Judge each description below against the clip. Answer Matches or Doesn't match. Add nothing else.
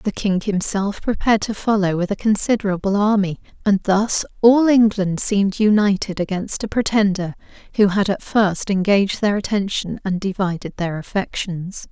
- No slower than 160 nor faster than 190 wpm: Doesn't match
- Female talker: Matches